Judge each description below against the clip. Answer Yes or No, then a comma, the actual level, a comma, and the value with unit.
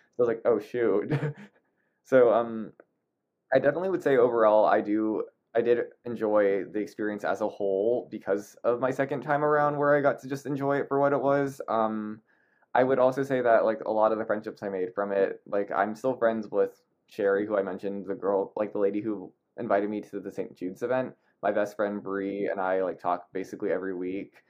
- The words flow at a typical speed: No, fast, 215 wpm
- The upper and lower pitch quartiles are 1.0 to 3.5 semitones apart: No, average, 4.6 semitones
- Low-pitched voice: Yes, low, 110 Hz